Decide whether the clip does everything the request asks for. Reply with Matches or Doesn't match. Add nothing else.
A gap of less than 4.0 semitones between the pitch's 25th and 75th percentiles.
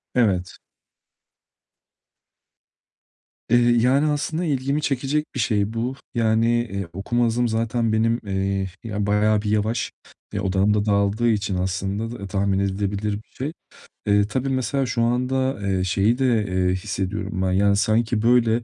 Matches